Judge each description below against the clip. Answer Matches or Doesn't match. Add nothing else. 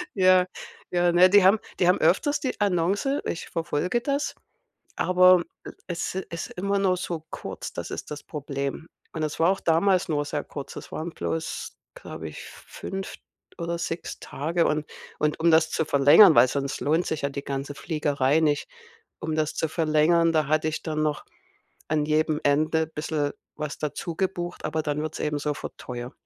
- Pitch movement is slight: Doesn't match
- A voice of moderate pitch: Matches